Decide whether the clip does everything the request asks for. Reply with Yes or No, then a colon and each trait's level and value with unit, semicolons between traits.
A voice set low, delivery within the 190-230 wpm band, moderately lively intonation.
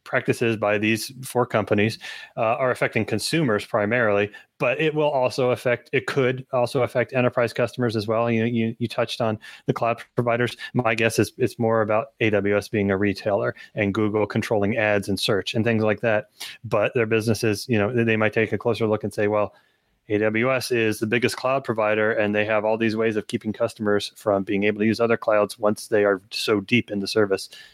No: low, 110 Hz; fast, 205 wpm; narrow, 2.1 semitones